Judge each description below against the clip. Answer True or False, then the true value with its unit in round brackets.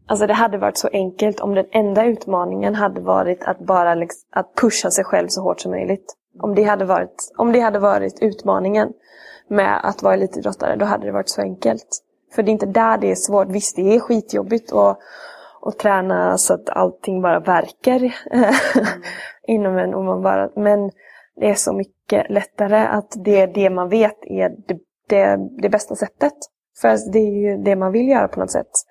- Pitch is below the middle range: False (205 Hz)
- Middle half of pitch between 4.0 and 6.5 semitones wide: False (3.0 semitones)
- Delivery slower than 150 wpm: False (200 wpm)